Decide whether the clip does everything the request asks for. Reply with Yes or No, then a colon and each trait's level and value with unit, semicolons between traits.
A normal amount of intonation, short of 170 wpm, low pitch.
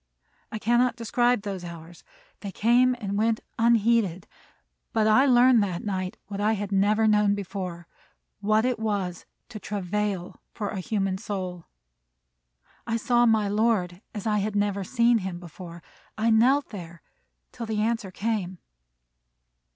No: average, 3.2 semitones; average, 145 wpm; high, 210 Hz